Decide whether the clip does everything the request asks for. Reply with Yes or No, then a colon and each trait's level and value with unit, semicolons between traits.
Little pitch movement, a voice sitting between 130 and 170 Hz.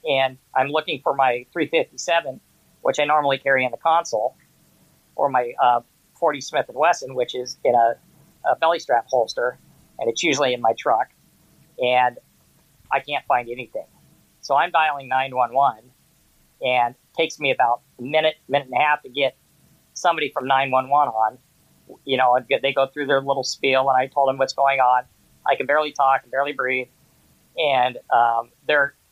Yes: narrow, 2.2 semitones; low, 135 Hz